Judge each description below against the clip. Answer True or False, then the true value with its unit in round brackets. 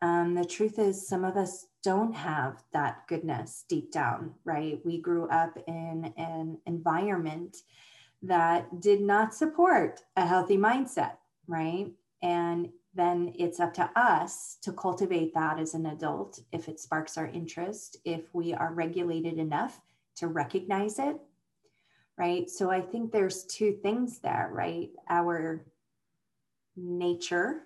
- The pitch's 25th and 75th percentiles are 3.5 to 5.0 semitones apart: False (3.0 semitones)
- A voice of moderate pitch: True (175 Hz)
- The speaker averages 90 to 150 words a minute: True (140 wpm)